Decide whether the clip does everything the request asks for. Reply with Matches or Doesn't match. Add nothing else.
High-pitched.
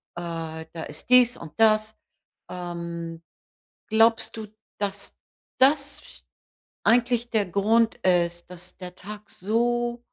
Matches